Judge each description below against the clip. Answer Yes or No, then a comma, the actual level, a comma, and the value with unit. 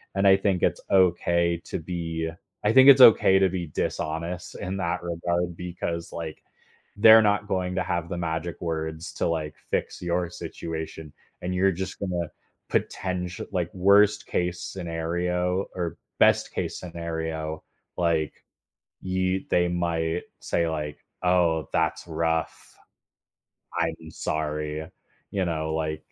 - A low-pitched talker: Yes, very low, 85 Hz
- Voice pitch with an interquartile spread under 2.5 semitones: Yes, narrow, 2.1 semitones